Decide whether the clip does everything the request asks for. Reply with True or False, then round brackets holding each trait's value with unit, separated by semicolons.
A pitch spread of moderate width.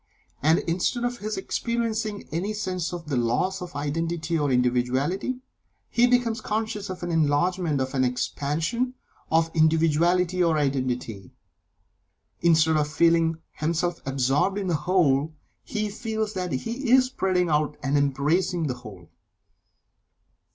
True (5.0 semitones)